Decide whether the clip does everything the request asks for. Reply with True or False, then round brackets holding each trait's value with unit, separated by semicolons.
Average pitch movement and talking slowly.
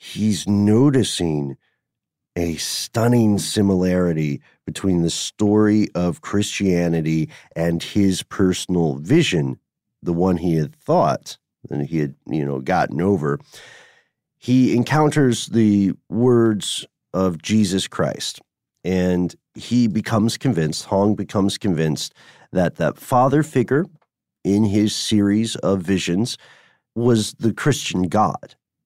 True (4.4 semitones; 110 wpm)